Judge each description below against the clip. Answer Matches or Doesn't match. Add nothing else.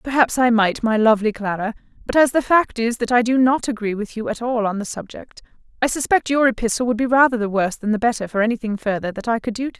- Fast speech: Matches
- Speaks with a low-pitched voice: Doesn't match